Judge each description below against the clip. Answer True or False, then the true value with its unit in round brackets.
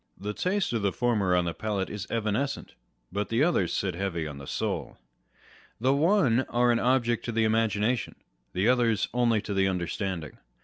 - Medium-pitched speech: False (110 Hz)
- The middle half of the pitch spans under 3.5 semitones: False (4.1 semitones)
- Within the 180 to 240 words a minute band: True (185 wpm)